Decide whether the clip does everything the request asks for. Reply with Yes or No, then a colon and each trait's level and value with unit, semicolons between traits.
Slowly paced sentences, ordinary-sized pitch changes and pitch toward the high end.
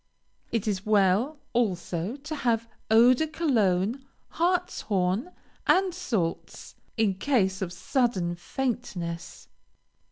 No: slow, 100 wpm; wide, 6.4 semitones; high, 225 Hz